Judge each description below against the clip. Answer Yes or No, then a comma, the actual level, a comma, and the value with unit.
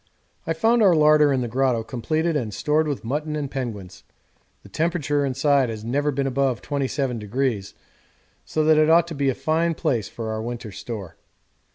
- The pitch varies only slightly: No, average, 4.4 semitones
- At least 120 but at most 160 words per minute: No, average, 180 wpm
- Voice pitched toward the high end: No, medium, 140 Hz